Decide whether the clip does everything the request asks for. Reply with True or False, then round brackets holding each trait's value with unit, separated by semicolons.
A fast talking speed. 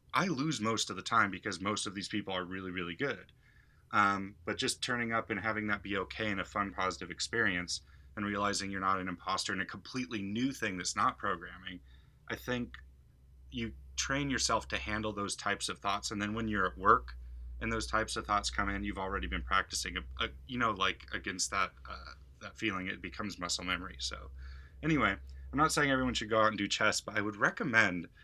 True (215 wpm)